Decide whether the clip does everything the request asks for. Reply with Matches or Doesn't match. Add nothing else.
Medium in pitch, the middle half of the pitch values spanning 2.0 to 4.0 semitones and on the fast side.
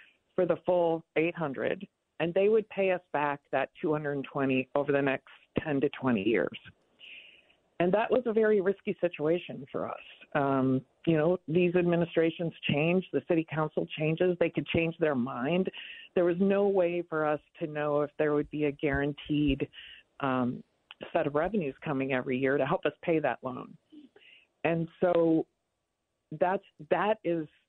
Doesn't match